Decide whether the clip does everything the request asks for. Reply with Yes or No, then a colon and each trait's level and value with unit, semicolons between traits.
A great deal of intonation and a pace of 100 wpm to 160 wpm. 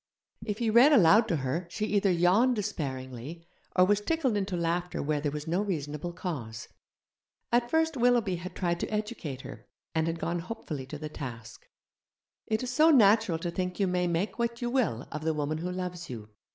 No: wide, 5.8 semitones; average, 195 wpm